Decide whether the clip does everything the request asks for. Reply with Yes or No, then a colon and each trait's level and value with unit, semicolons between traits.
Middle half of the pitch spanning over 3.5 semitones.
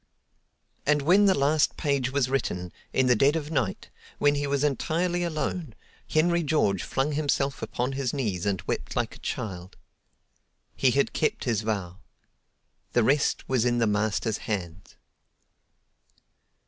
Yes: average, 5.3 semitones